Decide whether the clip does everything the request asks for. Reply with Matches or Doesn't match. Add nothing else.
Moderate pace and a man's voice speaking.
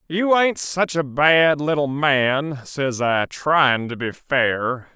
Matches